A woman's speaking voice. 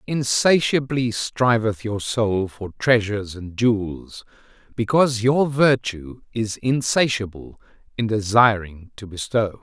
No: male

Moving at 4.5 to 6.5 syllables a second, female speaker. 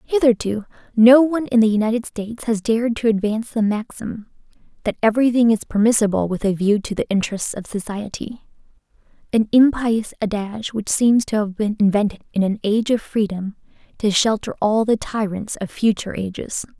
Yes: 5.7 syllables/s; female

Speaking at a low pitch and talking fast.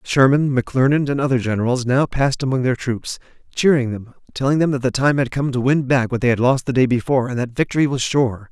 Yes: low, 130 Hz; fast, 240 wpm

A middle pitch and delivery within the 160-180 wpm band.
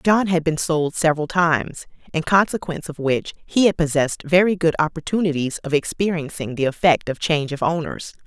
Yes: medium, 160 Hz; average, 175 wpm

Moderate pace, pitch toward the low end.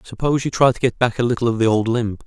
No: fast, 320 wpm; low, 120 Hz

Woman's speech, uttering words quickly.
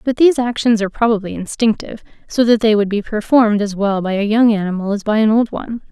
Yes: female; fast, 235 wpm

